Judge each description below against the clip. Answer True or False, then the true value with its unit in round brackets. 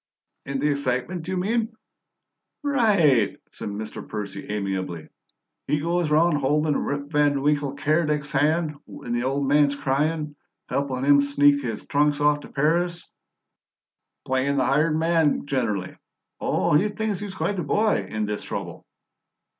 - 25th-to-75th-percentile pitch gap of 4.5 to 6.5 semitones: False (3.3 semitones)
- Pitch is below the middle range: False (145 Hz)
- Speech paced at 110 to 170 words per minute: True (145 wpm)